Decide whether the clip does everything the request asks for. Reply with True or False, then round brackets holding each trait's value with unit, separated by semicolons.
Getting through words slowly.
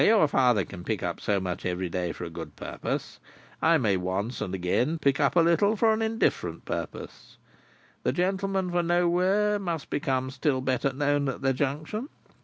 False (190 wpm)